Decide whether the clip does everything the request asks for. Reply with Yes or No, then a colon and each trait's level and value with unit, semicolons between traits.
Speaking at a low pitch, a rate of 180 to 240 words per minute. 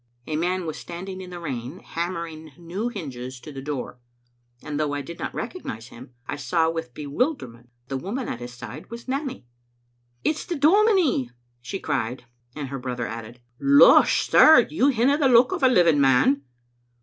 No: medium, 155 Hz; average, 190 wpm